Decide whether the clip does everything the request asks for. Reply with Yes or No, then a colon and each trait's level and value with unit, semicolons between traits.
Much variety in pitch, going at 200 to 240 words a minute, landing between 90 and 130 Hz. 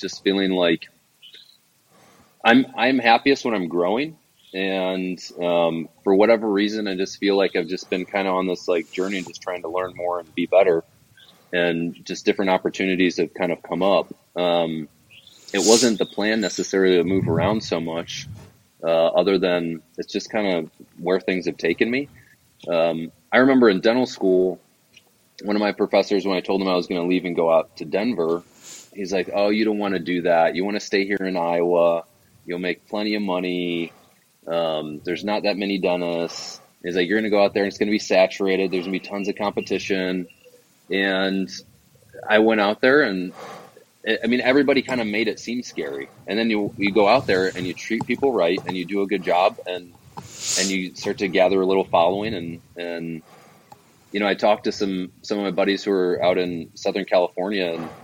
No: average, 2.9 semitones; fast, 205 wpm; very low, 95 Hz